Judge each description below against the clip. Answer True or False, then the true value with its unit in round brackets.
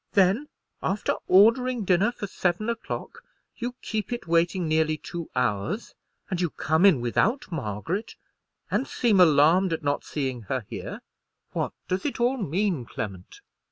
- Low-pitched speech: False (180 Hz)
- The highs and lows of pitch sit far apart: True (6.0 semitones)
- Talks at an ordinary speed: True (150 wpm)